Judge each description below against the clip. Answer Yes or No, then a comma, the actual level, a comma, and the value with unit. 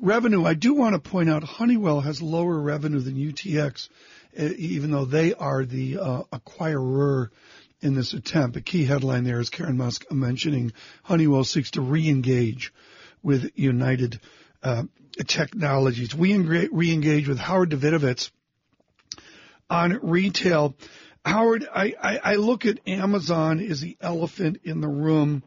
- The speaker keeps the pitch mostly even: No, average, 4.1 semitones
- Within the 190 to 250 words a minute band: No, average, 140 wpm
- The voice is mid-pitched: Yes, medium, 155 Hz